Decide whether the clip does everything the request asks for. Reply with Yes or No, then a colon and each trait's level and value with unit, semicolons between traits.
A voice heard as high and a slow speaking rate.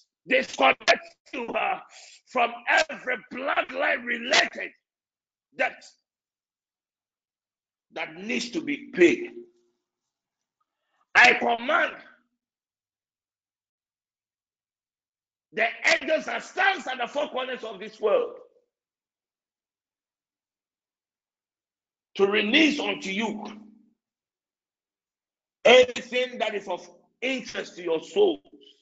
Yes: high, 235 Hz; slow, 80 wpm